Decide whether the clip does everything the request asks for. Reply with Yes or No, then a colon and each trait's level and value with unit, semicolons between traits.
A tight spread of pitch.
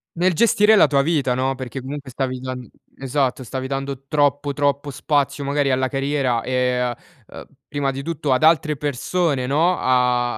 Yes: narrow, 2.2 semitones